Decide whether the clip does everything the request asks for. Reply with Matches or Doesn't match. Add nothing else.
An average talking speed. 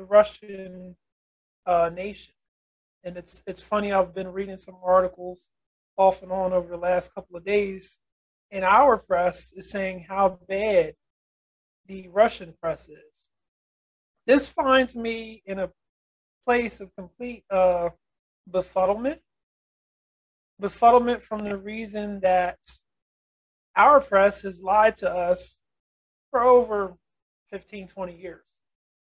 Doesn't match